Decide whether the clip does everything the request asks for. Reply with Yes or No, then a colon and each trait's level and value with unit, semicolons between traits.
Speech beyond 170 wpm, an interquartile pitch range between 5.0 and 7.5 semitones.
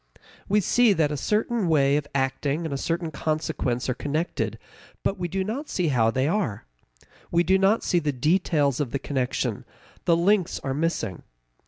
Yes: average, 180 wpm; average, 5.3 semitones